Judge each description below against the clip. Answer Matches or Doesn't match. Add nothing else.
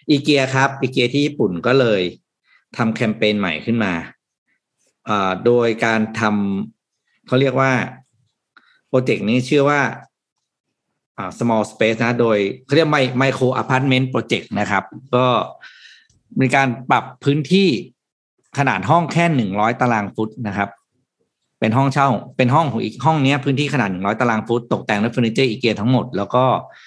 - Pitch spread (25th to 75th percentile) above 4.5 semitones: Doesn't match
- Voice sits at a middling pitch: Doesn't match